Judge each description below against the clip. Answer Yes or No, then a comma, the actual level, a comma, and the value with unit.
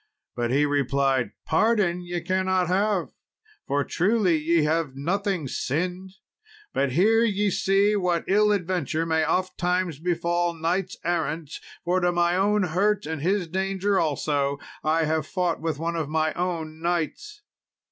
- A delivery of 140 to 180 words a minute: Yes, average, 145 wpm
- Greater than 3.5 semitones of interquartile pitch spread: No, average, 3.2 semitones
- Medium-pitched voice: Yes, medium, 175 Hz